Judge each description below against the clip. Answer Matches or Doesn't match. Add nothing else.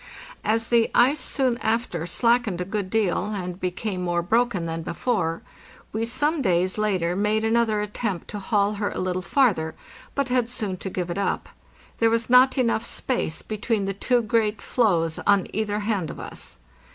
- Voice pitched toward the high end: Matches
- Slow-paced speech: Doesn't match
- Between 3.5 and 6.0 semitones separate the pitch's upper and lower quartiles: Matches